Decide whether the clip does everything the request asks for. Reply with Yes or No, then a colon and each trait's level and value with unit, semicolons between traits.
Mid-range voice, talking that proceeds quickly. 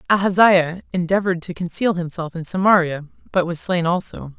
No: medium, 175 Hz; average, 150 wpm